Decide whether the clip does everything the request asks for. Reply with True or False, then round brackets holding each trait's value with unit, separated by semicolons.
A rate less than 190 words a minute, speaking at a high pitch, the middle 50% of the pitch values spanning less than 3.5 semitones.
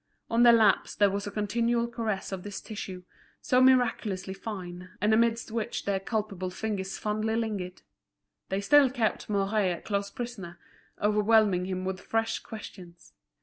True (150 wpm; 210 Hz; 2.9 semitones)